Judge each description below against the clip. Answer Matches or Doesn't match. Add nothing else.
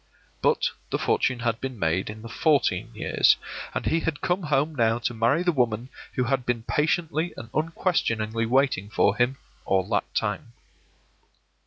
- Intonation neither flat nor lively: Matches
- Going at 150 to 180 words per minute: Matches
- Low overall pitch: Matches